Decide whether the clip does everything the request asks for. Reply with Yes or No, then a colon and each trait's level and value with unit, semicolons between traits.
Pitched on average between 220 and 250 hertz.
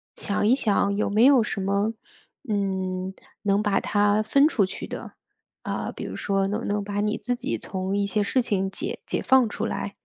No: high, 205 Hz